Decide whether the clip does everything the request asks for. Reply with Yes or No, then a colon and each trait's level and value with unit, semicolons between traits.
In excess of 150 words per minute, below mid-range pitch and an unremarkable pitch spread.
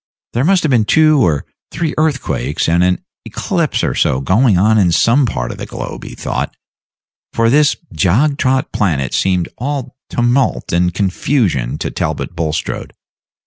No: average, 160 wpm; low, 110 Hz; wide, 7.8 semitones